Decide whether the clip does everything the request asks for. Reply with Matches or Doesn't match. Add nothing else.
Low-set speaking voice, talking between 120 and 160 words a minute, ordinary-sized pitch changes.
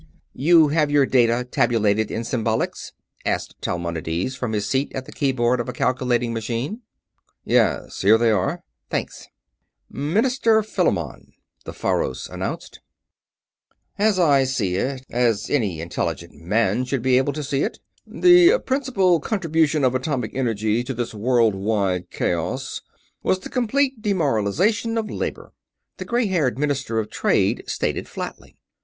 Doesn't match